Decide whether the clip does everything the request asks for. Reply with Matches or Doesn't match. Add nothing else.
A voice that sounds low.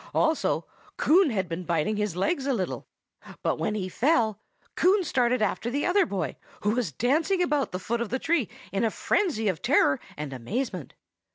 Doesn't match